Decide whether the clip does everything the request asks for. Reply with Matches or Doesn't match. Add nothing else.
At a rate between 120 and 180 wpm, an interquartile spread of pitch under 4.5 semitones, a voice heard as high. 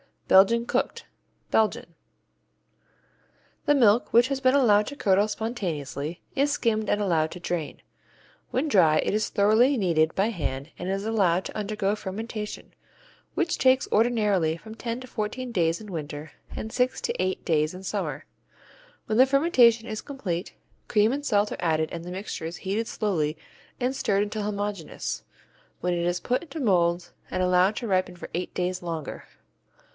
Doesn't match